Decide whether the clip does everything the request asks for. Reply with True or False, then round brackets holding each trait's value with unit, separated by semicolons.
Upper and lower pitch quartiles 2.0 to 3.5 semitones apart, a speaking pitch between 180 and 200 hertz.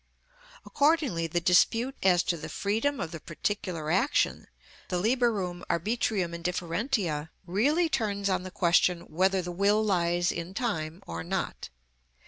False (4.3 semitones; 185 Hz)